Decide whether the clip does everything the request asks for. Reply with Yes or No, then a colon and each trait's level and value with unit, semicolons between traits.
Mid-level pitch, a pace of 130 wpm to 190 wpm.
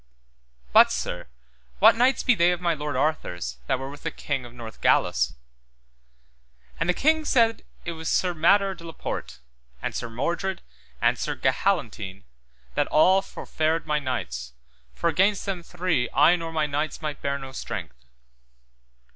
Yes: medium, 155 Hz; average, 165 wpm